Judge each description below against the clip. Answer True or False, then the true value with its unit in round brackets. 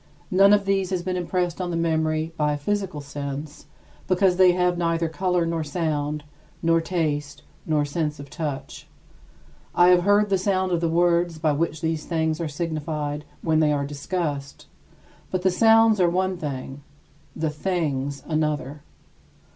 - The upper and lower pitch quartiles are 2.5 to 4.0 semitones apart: True (3.3 semitones)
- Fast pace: False (165 wpm)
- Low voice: False (165 Hz)